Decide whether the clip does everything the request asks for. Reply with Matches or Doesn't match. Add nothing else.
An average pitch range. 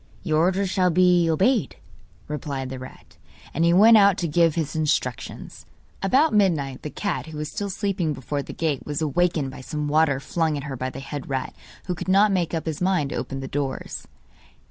Matches